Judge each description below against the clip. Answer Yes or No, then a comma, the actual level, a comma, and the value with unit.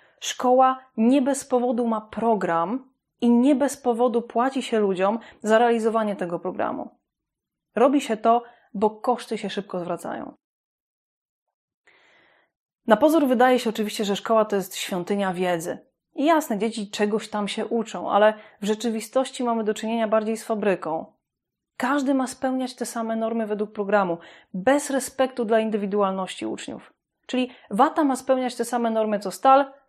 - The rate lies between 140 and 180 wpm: Yes, average, 150 wpm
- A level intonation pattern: No, average, 3.5 semitones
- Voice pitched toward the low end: No, high, 225 Hz